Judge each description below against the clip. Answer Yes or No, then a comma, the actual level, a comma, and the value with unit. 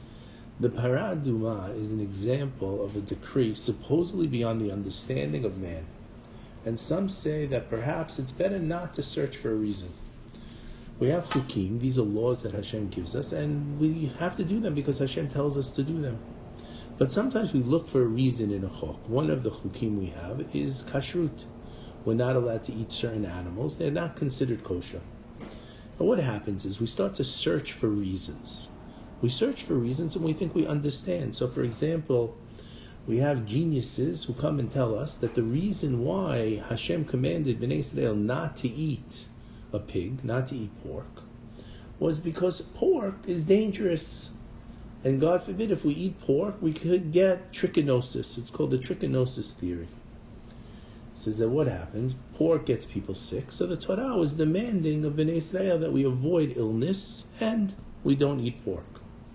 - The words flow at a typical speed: Yes, average, 175 wpm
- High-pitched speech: No, low, 125 Hz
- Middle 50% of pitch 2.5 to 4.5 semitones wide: No, wide, 5.6 semitones